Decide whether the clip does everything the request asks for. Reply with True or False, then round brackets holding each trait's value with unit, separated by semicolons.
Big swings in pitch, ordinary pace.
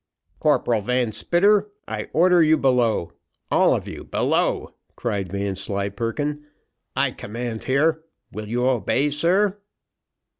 False (6.7 semitones; 115 wpm)